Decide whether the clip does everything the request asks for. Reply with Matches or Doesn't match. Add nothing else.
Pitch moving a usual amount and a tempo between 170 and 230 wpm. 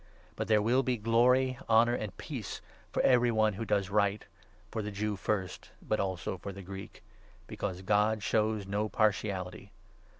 Doesn't match